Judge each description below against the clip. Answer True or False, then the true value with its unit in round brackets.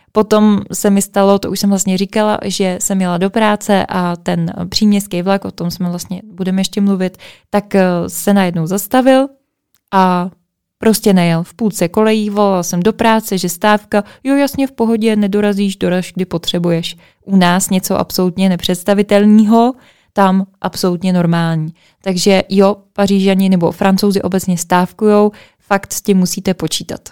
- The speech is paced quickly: False (155 wpm)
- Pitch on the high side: True (195 Hz)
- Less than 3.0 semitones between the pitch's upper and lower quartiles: True (2.4 semitones)